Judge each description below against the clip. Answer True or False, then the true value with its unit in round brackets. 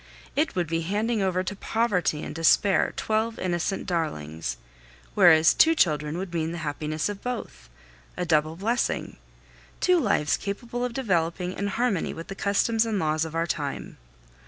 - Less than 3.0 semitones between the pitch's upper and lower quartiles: False (4.8 semitones)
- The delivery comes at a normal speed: True (160 wpm)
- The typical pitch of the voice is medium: True (180 Hz)